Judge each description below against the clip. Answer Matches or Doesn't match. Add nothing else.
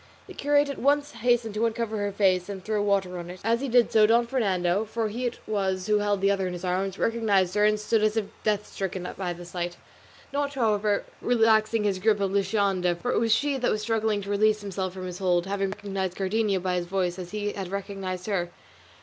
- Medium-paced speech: Doesn't match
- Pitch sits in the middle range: Doesn't match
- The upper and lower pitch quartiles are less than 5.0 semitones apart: Matches